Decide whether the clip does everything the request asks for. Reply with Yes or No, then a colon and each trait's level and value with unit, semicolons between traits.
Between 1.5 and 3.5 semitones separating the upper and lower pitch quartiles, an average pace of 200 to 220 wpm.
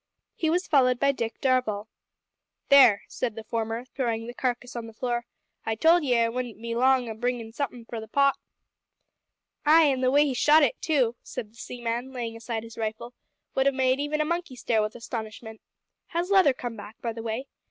Yes: average, 3.2 semitones; fast, 205 wpm